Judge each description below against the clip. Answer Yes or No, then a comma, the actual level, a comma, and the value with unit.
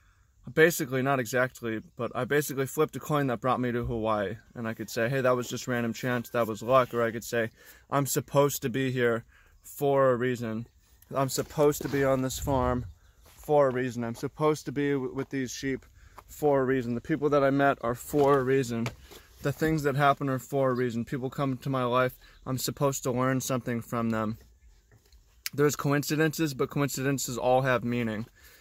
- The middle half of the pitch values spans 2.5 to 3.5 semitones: Yes, average, 3.1 semitones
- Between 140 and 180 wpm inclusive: No, average, 200 wpm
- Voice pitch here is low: Yes, low, 130 Hz